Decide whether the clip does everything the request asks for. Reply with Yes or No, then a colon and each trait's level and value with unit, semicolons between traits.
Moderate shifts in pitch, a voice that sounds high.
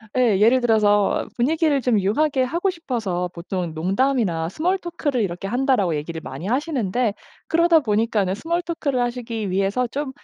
No: wide, 6.2 semitones; high, 235 Hz